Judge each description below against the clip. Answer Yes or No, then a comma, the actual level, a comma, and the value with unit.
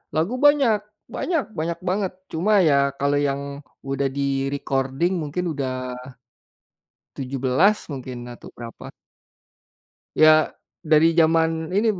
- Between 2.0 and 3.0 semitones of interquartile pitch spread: No, average, 4.6 semitones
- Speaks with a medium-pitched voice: Yes, medium, 155 Hz